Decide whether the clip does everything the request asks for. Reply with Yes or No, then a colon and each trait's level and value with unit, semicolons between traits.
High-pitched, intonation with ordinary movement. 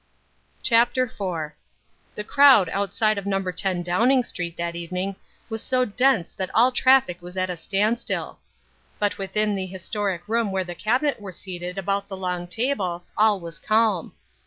Yes: high, 195 Hz; average, 3.7 semitones